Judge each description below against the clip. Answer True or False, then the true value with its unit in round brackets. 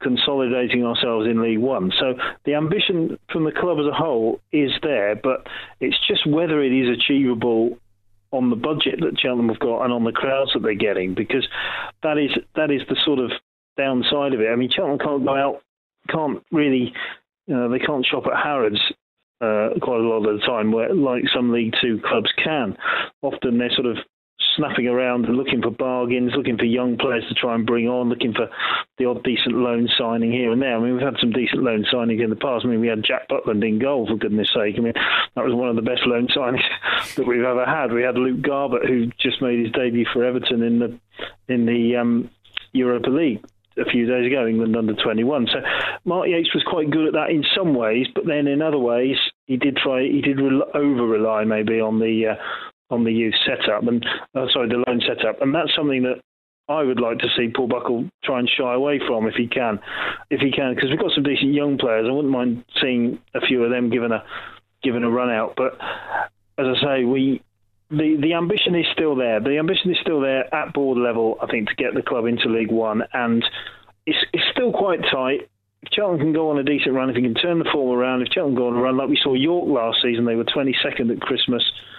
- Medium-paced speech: False (230 wpm)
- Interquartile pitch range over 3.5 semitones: False (3.1 semitones)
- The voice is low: True (125 Hz)